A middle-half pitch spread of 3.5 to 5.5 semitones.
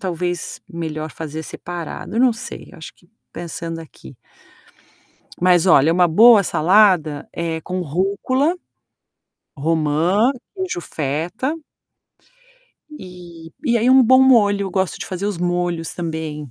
Yes: average, 4.0 semitones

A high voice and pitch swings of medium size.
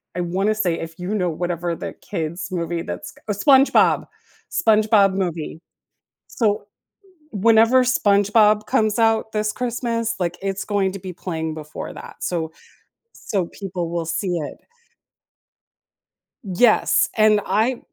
Yes: high, 195 Hz; average, 3.8 semitones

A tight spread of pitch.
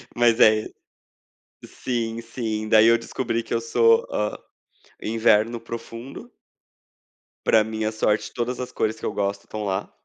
Yes: narrow, 1.3 semitones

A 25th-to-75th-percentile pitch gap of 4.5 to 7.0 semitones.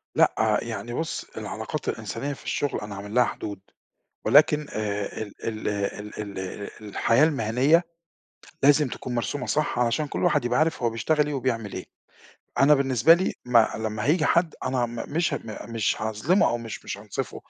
Yes: average, 5.2 semitones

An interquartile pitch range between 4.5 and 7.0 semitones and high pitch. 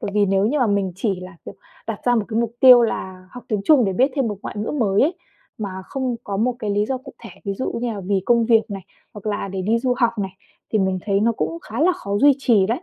No: average, 3.7 semitones; high, 220 Hz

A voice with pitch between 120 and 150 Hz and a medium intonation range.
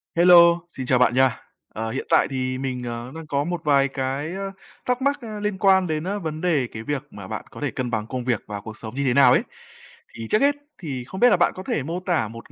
No: medium, 140 Hz; wide, 6.3 semitones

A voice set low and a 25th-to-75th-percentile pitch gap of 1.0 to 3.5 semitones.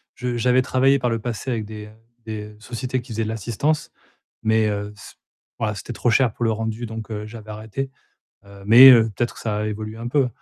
Yes: low, 115 Hz; narrow, 2.4 semitones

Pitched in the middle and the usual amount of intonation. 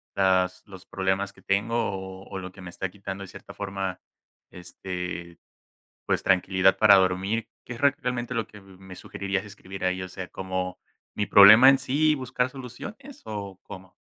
No: very low, 95 Hz; average, 3.4 semitones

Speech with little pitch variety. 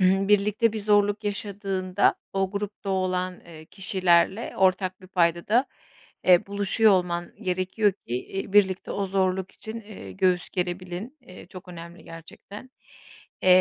Yes: narrow, 1.9 semitones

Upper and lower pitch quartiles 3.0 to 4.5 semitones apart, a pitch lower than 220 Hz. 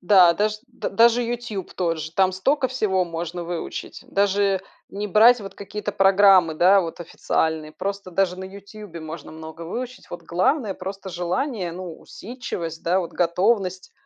Yes: average, 3.3 semitones; high, 190 Hz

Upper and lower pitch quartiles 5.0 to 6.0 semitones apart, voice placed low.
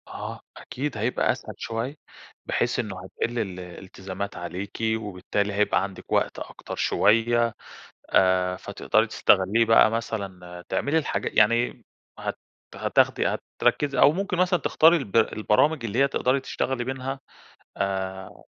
Yes: wide, 5.4 semitones; low, 110 Hz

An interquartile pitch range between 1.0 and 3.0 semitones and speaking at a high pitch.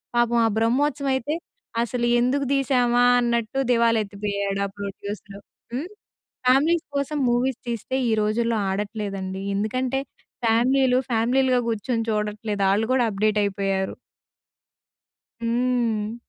No: average, 3.4 semitones; high, 235 Hz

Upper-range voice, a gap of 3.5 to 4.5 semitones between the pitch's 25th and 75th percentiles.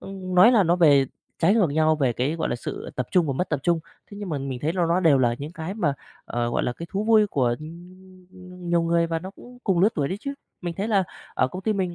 No: medium, 170 Hz; average, 4.2 semitones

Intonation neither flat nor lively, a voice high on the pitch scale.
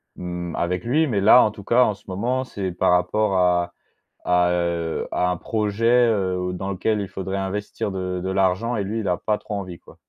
No: average, 3.1 semitones; very low, 95 Hz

